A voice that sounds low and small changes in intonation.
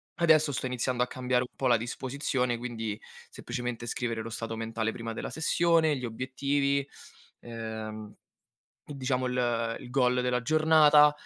No: low, 125 Hz; average, 3.3 semitones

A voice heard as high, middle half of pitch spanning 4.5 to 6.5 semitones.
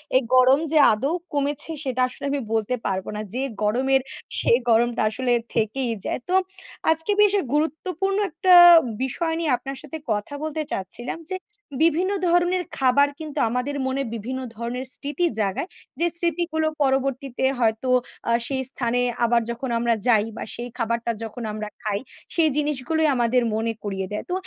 Yes: very high, 260 Hz; average, 4.9 semitones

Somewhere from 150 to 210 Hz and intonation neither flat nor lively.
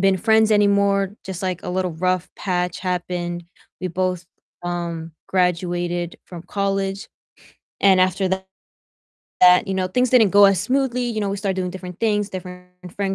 No: medium, 185 Hz; narrow, 2.0 semitones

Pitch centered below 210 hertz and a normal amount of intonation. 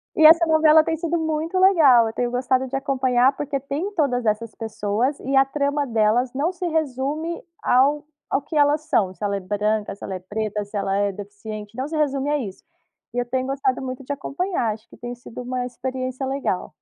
No: very high, 260 Hz; average, 4.9 semitones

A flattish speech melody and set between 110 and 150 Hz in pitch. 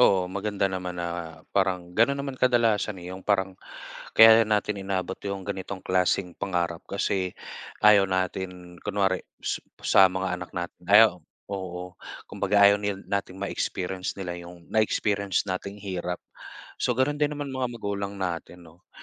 No: narrow, 2.1 semitones; very low, 95 Hz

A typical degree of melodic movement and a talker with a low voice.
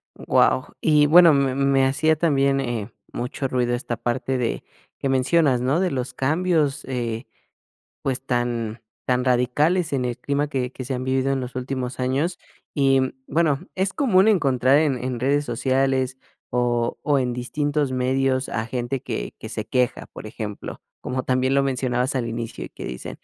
No: narrow, 2.2 semitones; low, 130 Hz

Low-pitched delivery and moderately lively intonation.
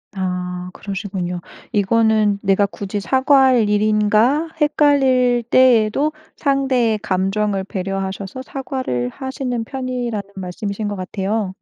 No: high, 215 Hz; average, 4.8 semitones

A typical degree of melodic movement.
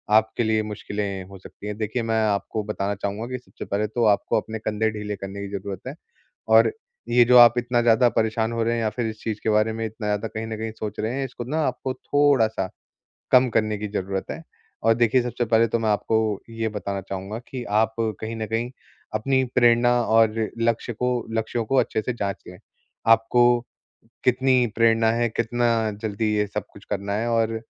No: narrow, 2.0 semitones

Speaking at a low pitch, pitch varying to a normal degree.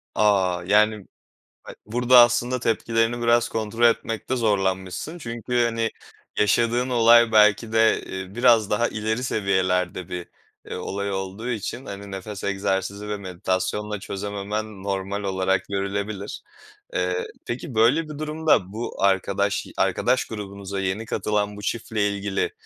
Yes: low, 105 Hz; average, 3.1 semitones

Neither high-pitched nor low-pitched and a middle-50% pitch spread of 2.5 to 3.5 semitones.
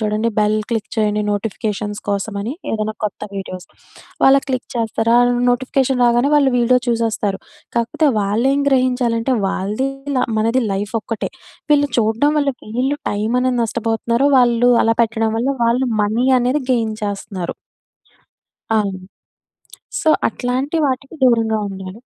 No: high, 230 Hz; average, 3.2 semitones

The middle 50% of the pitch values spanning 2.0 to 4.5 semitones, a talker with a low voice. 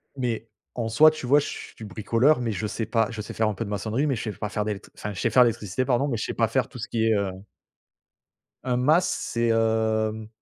Yes: narrow, 2.5 semitones; low, 115 Hz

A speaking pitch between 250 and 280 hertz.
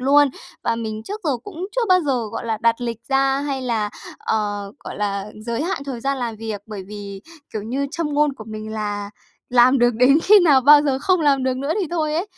Yes: very high, 255 Hz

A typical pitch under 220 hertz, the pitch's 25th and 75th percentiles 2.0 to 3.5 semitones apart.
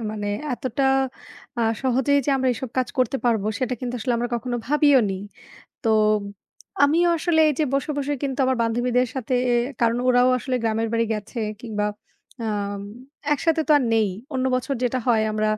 No: very high, 250 Hz; average, 3.1 semitones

